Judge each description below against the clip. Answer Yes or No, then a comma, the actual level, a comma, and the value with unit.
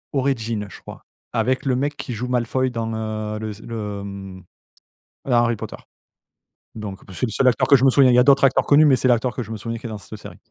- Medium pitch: No, low, 115 Hz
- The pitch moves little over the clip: No, average, 3.2 semitones